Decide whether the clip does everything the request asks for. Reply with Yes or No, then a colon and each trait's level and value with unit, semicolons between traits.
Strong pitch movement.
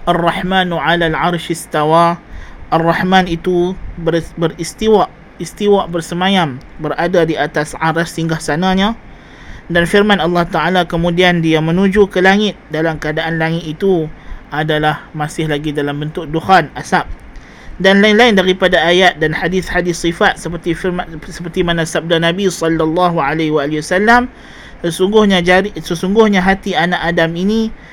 No: narrow, 2.4 semitones